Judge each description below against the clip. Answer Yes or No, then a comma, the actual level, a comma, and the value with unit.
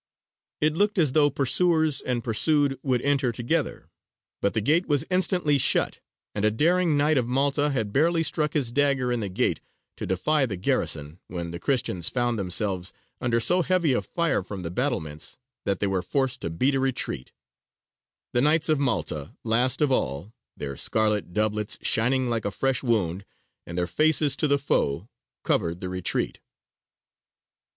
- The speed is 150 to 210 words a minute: Yes, average, 170 wpm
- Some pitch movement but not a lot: No, wide, 6.4 semitones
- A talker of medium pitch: No, low, 125 Hz